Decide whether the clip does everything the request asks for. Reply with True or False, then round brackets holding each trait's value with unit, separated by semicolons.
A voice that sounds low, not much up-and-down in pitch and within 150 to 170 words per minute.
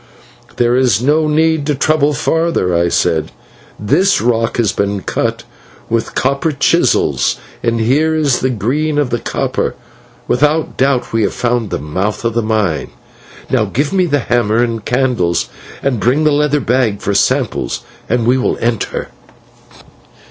False (125 Hz; 4.8 semitones; 155 wpm)